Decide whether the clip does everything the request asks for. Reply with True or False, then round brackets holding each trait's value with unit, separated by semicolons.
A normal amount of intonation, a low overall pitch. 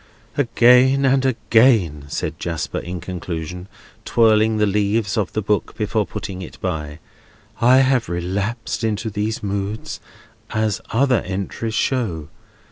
True (4.0 semitones; 105 Hz)